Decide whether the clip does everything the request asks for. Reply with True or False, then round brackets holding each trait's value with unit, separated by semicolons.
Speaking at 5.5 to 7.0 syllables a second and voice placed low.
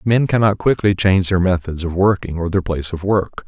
True (5.9 syllables/s; 95 Hz)